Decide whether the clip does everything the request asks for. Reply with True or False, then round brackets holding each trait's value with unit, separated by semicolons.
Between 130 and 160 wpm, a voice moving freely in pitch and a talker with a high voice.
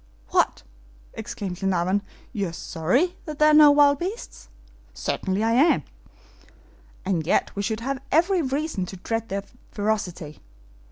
True (135 wpm; 7.6 semitones; 220 Hz)